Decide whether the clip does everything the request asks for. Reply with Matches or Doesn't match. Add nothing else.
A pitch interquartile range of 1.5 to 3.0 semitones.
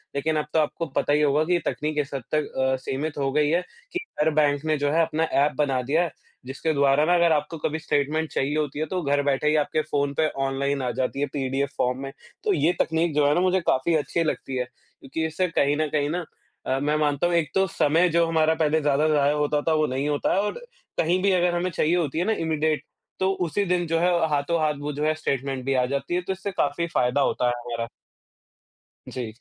Matches